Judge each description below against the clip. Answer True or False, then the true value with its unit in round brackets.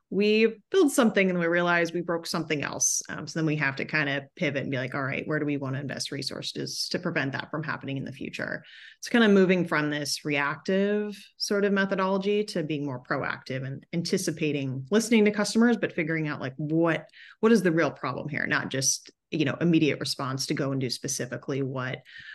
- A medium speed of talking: False (220 wpm)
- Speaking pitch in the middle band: True (155 Hz)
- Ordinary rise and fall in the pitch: False (5.8 semitones)